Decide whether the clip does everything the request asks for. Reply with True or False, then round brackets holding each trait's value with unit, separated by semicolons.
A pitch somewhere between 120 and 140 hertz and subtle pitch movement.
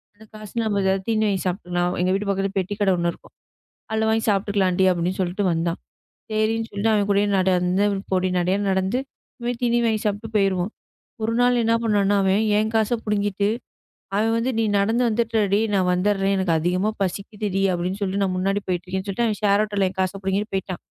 False (200 Hz; 2.3 semitones)